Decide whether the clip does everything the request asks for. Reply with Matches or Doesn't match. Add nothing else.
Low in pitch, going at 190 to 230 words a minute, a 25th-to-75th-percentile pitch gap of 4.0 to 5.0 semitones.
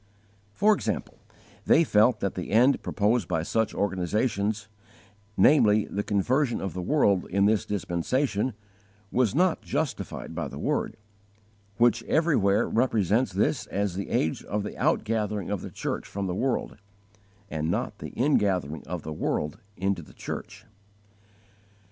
Doesn't match